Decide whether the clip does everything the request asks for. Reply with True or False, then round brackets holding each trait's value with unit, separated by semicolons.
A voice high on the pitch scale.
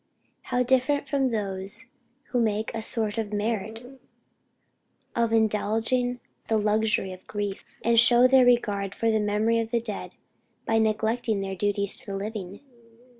True (220 Hz)